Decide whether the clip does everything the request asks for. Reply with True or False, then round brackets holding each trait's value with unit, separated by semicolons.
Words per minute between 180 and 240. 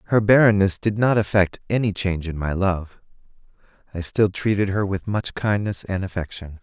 False (170 wpm)